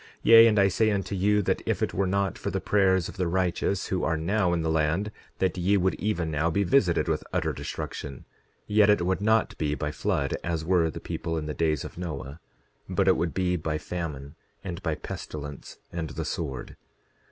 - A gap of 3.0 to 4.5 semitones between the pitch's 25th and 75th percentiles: Yes, average, 3.6 semitones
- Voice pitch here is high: No, very low, 90 Hz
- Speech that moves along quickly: Yes, fast, 215 wpm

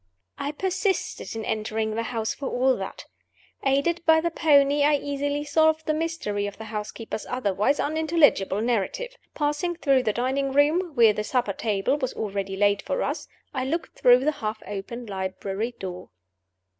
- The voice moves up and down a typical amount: No, wide, 5.8 semitones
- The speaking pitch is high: Yes, very high, 255 Hz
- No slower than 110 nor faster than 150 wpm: No, average, 165 wpm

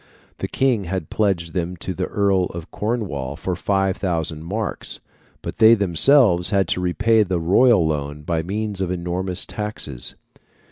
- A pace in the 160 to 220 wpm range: No, average, 150 wpm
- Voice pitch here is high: No, very low, 95 Hz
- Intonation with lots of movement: No, average, 3.8 semitones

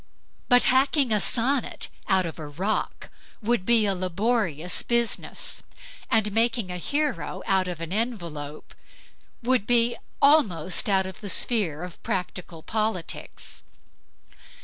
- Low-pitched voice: No, high, 205 Hz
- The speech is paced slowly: Yes, slow, 125 wpm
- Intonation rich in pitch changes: No, average, 4.8 semitones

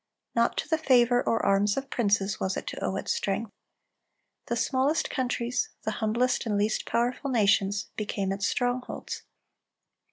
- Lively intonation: No, average, 3.7 semitones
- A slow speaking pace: No, average, 155 wpm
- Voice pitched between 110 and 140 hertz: No, high, 230 Hz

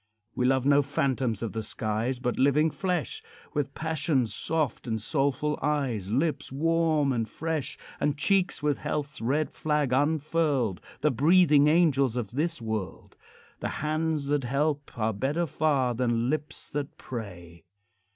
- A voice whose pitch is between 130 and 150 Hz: Yes, medium, 140 Hz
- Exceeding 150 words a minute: No, average, 145 wpm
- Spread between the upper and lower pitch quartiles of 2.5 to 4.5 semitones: Yes, average, 3.9 semitones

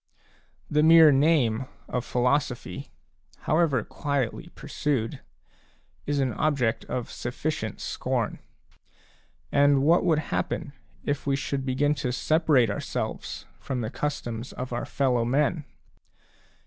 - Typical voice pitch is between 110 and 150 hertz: Yes, medium, 140 Hz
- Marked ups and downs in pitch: No, average, 3.3 semitones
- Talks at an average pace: No, slow, 110 wpm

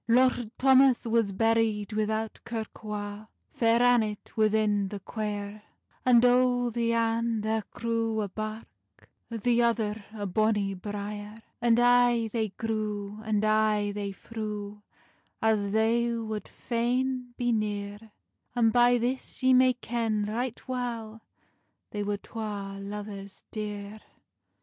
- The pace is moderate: No, slow, 125 wpm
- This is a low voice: No, high, 220 Hz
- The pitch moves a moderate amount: No, narrow, 2.2 semitones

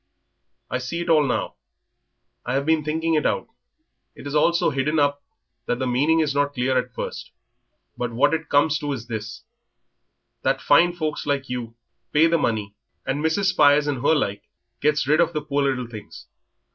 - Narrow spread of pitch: No, average, 3.5 semitones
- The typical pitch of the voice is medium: Yes, medium, 145 Hz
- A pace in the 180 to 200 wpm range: Yes, average, 190 wpm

